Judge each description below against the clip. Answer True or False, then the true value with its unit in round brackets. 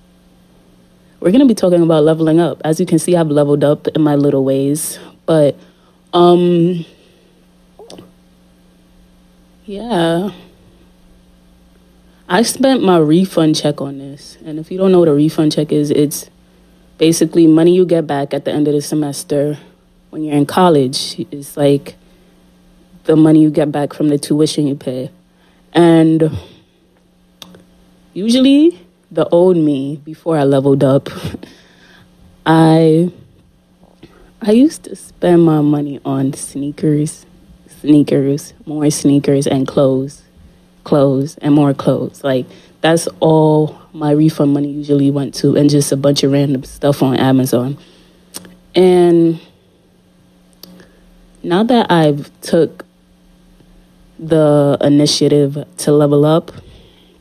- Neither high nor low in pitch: True (145 Hz)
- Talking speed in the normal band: False (130 wpm)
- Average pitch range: True (4.2 semitones)